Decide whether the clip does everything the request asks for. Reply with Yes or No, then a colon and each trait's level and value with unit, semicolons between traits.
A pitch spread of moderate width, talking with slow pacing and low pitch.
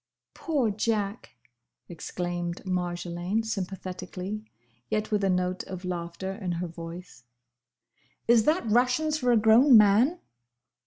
No: average, 4.1 semitones; slow, 115 wpm; high, 195 Hz